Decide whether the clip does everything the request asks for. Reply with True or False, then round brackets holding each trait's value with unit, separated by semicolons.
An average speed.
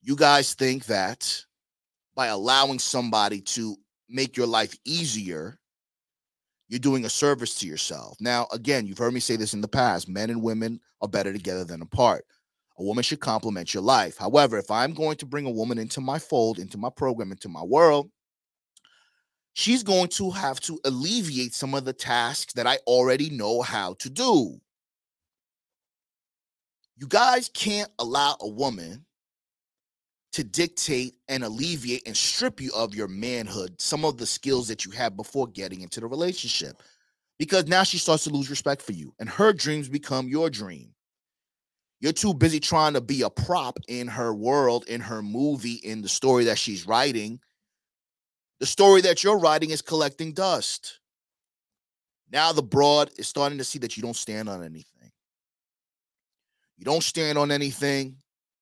True (170 wpm)